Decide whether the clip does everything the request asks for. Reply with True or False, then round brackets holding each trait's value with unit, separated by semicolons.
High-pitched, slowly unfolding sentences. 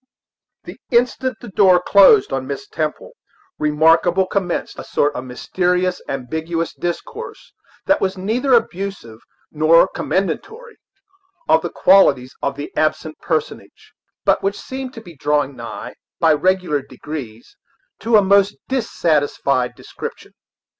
False (175 Hz; 125 wpm)